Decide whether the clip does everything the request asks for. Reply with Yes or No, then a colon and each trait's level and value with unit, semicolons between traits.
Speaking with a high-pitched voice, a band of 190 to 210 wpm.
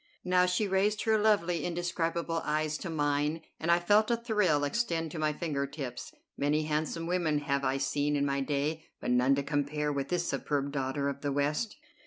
No: medium, 155 Hz; average, 195 wpm